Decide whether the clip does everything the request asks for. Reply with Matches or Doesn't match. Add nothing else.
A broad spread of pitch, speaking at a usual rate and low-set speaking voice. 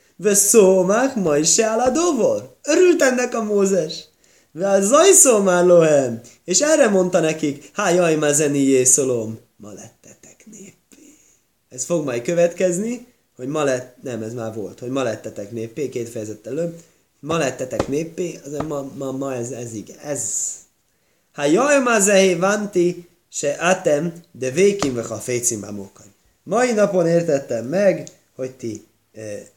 Doesn't match